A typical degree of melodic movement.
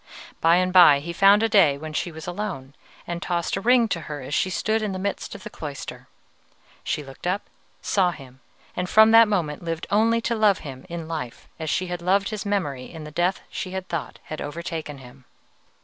Yes: average, 4.8 semitones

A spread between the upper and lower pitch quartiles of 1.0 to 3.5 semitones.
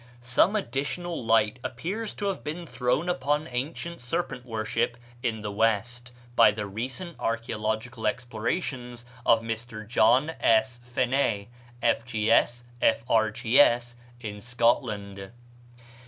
Yes: average, 3.0 semitones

